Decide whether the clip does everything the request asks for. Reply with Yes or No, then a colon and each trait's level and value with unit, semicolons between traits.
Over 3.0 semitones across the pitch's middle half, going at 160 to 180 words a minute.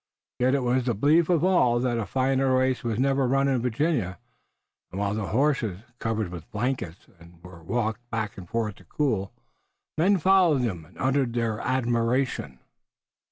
Yes: average, 4.0 semitones; average, 165 wpm